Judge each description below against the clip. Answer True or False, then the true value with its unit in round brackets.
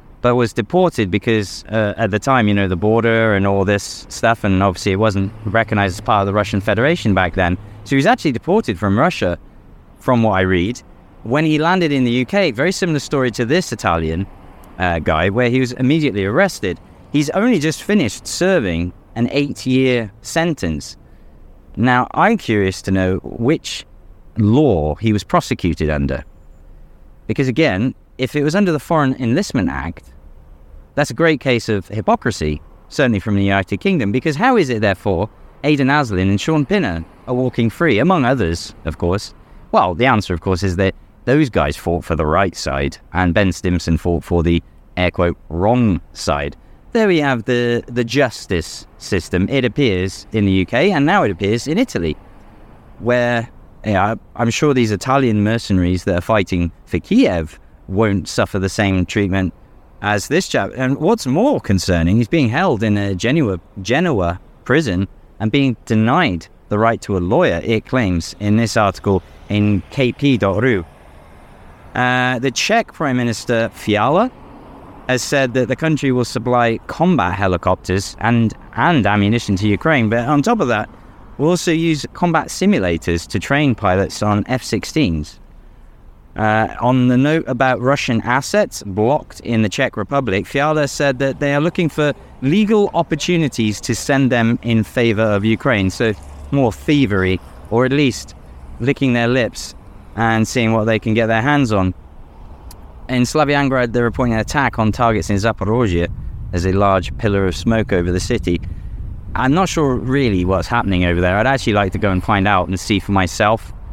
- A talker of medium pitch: False (110 Hz)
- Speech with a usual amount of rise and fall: False (5.8 semitones)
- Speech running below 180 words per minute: True (170 wpm)